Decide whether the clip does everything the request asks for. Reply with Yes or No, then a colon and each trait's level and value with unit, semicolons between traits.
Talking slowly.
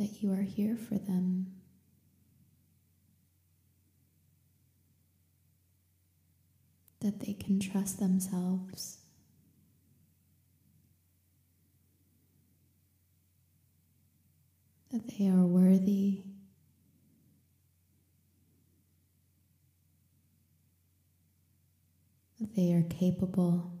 Yes: slow, 50 wpm